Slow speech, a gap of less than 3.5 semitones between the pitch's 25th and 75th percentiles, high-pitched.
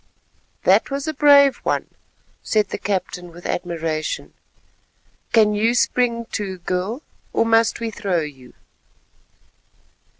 No: slow, 120 wpm; average, 4.8 semitones; high, 210 Hz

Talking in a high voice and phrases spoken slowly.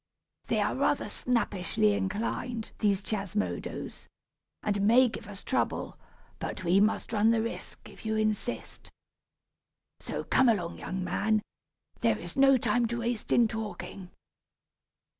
Yes: high, 215 Hz; slow, 130 wpm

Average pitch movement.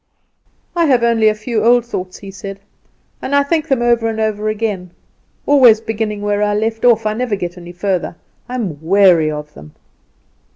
Yes: average, 3.4 semitones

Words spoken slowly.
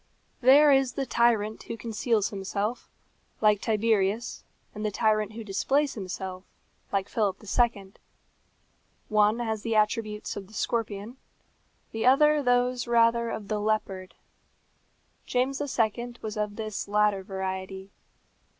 Yes: slow, 125 wpm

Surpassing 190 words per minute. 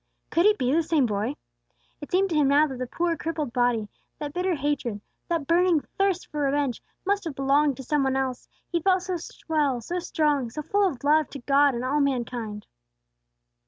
Yes: average, 200 wpm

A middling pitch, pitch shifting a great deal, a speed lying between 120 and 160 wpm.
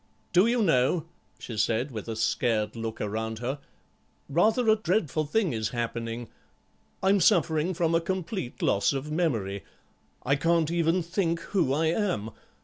Yes: medium, 155 Hz; wide, 7.3 semitones; average, 150 wpm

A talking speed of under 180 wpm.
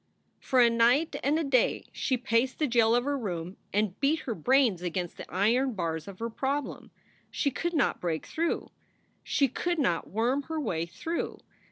No: average, 185 wpm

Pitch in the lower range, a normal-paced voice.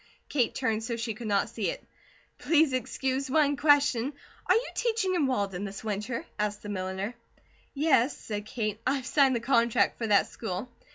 No: high, 235 Hz; average, 180 wpm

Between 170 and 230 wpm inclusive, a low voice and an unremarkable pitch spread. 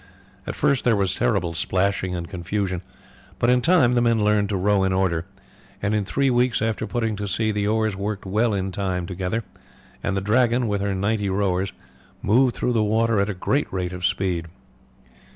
Yes: average, 195 wpm; low, 100 Hz; average, 3.1 semitones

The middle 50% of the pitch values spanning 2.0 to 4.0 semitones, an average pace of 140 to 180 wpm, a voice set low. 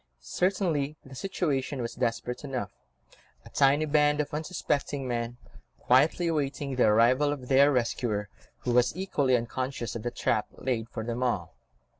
Yes: average, 3.4 semitones; average, 150 wpm; low, 130 Hz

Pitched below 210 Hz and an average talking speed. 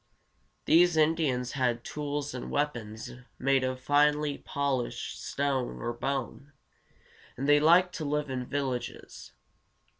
No: medium, 140 Hz; slow, 120 wpm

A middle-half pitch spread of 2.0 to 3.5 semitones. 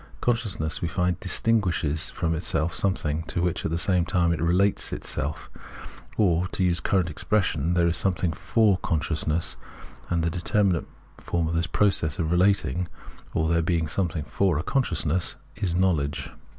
Yes: narrow, 2.5 semitones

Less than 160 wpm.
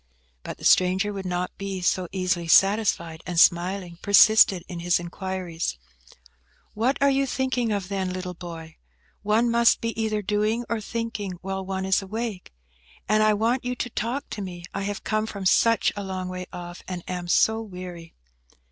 No: average, 175 wpm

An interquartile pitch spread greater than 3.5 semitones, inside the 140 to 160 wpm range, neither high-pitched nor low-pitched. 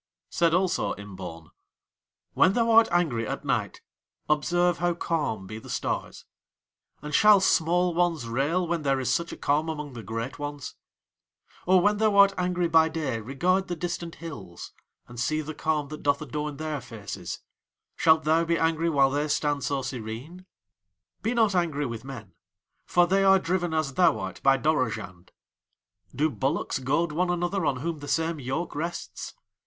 No: average, 4.5 semitones; average, 170 wpm; medium, 155 Hz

